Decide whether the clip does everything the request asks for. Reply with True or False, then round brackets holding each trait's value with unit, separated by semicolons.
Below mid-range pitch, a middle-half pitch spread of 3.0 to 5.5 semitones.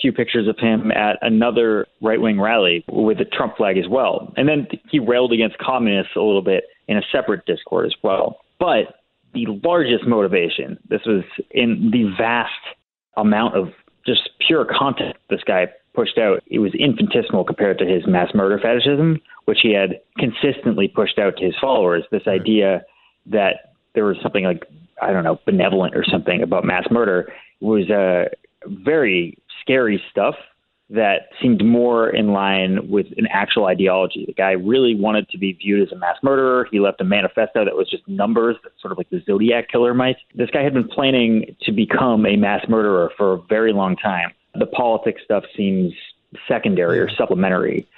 True (115 Hz; 4.4 semitones)